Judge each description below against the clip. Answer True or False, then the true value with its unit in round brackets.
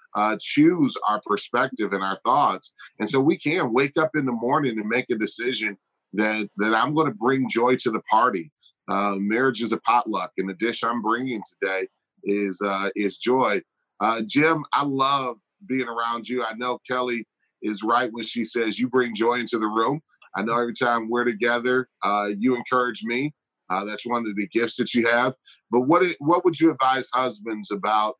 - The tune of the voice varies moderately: True (3.3 semitones)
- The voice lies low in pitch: True (120 Hz)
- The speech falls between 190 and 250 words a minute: True (200 wpm)